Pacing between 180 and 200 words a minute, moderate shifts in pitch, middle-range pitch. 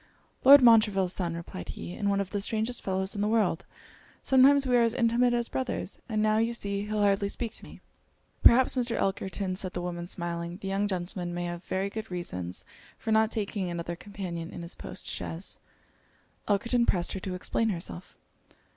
No: average, 190 wpm; average, 4.1 semitones; high, 200 Hz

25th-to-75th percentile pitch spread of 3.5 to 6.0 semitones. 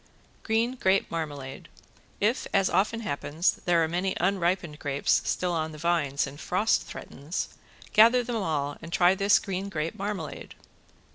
Yes: average, 4.4 semitones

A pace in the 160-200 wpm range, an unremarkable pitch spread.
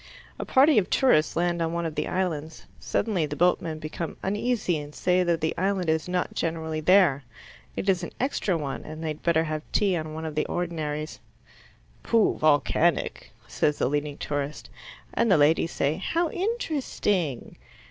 Yes: average, 175 wpm; average, 3.4 semitones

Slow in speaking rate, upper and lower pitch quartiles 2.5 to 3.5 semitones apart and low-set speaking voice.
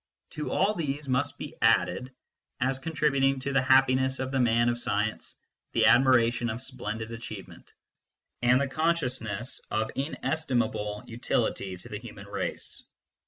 No: average, 145 wpm; average, 2.8 semitones; low, 130 Hz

